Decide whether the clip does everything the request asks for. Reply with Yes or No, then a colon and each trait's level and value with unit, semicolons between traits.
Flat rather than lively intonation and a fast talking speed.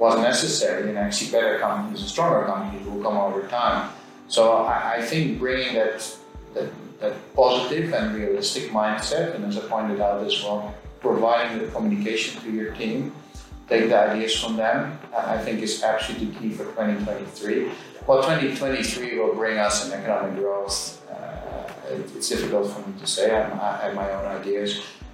No: narrow, 2.0 semitones; average, 165 wpm